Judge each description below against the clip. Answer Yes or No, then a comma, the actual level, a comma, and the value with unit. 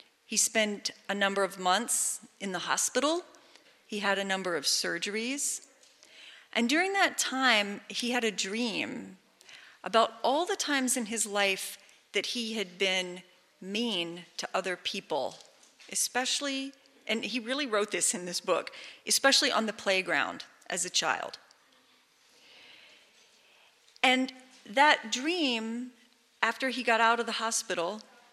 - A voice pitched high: Yes, high, 225 Hz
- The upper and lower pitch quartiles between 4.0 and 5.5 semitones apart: Yes, average, 4.5 semitones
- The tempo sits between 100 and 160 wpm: Yes, slow, 135 wpm